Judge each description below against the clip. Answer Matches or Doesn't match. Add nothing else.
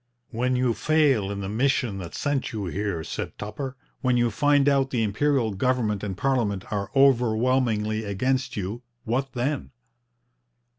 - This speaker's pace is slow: Doesn't match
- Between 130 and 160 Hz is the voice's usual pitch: Doesn't match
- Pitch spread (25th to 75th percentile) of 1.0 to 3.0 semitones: Doesn't match